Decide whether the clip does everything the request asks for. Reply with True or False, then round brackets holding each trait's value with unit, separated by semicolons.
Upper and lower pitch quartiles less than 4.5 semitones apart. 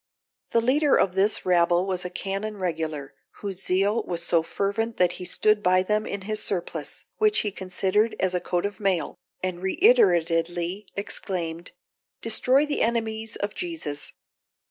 True (3.4 semitones)